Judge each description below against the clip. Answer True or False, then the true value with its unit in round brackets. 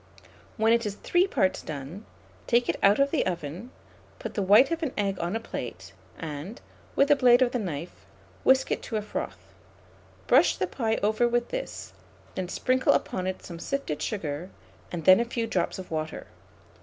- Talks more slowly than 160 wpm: False (190 wpm)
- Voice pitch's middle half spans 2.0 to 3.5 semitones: False (5.6 semitones)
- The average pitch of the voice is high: True (210 Hz)